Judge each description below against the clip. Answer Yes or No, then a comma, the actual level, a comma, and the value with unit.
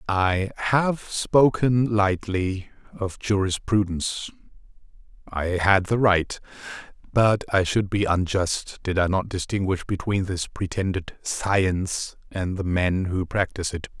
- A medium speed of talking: No, slow, 125 wpm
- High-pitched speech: No, very low, 95 Hz